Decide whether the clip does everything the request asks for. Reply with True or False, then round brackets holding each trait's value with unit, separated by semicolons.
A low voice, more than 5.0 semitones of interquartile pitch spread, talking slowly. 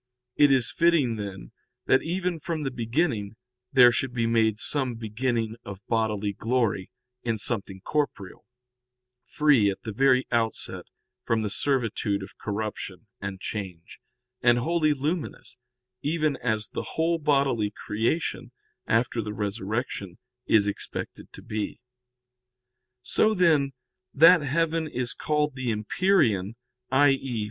True (120 Hz; 5.5 semitones; 125 wpm)